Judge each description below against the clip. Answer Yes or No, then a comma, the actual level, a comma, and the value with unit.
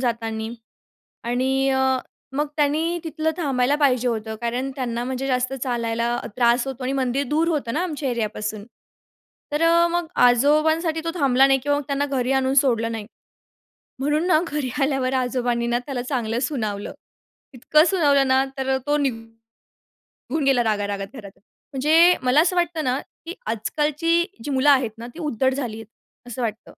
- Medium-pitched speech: No, very high, 265 Hz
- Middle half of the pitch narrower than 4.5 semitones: Yes, average, 3.8 semitones